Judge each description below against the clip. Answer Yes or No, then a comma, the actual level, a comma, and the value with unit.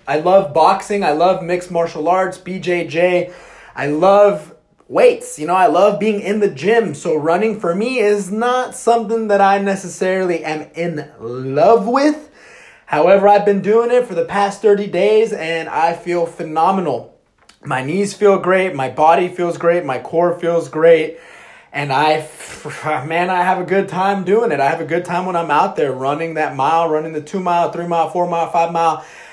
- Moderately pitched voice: Yes, medium, 175 Hz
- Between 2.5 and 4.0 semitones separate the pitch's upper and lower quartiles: Yes, average, 3.6 semitones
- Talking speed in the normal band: Yes, average, 190 wpm